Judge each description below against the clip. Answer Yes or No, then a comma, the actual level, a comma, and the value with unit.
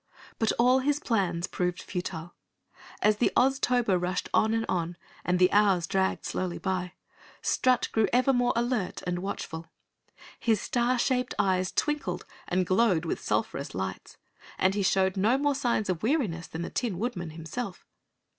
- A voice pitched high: Yes, high, 195 Hz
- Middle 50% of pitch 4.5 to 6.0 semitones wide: Yes, wide, 5.4 semitones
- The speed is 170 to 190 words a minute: No, average, 160 wpm